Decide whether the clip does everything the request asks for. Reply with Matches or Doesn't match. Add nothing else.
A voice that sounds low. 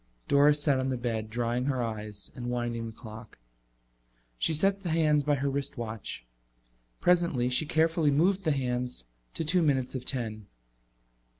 Matches